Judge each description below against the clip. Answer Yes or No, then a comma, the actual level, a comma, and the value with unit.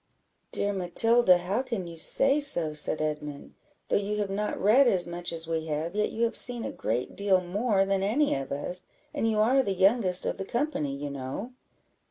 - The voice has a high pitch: Yes, high, 195 Hz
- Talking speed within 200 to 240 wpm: Yes, fast, 205 wpm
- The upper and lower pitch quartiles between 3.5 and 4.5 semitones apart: No, wide, 5.5 semitones